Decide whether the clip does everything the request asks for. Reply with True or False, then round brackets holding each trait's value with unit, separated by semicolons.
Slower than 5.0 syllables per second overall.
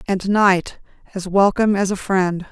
True (4.5 syllables/s)